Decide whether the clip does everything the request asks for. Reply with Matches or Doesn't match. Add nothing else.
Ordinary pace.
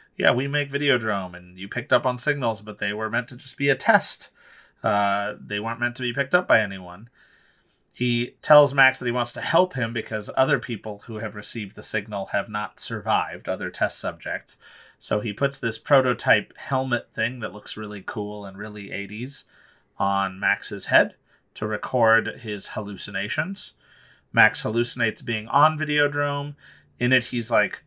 Matches